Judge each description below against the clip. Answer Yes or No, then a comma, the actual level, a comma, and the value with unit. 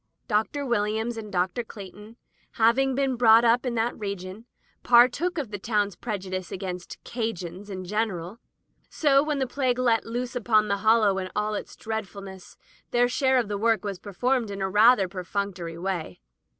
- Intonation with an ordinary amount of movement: Yes, average, 3.8 semitones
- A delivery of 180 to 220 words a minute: No, average, 170 wpm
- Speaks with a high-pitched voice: Yes, high, 215 Hz